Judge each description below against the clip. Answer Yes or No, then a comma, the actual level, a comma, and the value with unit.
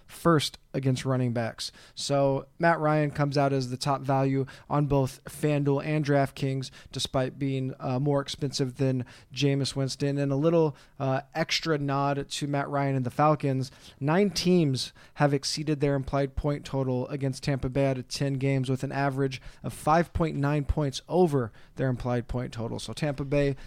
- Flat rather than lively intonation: Yes, narrow, 1.6 semitones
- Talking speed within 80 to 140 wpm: No, average, 165 wpm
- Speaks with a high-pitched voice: No, medium, 140 Hz